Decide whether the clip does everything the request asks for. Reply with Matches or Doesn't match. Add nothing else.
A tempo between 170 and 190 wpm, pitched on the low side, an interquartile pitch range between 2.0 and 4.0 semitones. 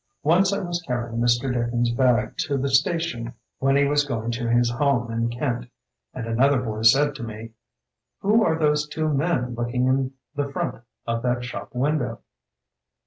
Matches